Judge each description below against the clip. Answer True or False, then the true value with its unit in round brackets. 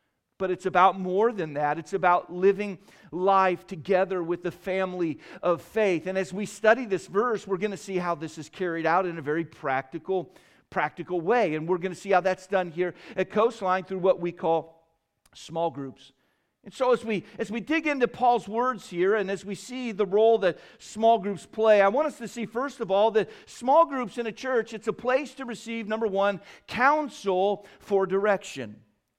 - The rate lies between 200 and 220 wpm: True (205 wpm)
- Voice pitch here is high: True (195 Hz)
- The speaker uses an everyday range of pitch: True (3.8 semitones)